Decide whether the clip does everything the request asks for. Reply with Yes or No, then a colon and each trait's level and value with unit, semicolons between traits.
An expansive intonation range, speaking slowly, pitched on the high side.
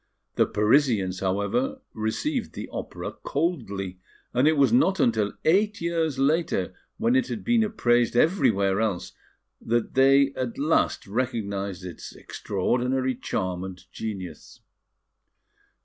No: wide, 8.4 semitones; slow, 120 wpm; low, 125 Hz